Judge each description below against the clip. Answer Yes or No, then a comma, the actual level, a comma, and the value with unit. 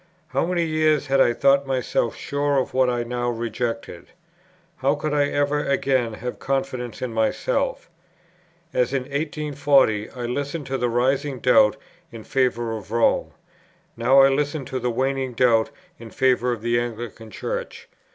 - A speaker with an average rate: Yes, average, 160 wpm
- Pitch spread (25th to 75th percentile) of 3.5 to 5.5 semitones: No, average, 3.0 semitones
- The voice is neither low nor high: No, low, 130 Hz